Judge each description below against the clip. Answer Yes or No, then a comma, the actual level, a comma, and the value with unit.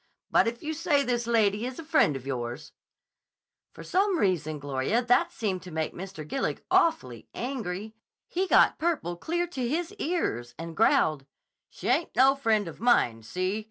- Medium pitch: No, high, 220 Hz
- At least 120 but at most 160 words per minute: No, average, 170 wpm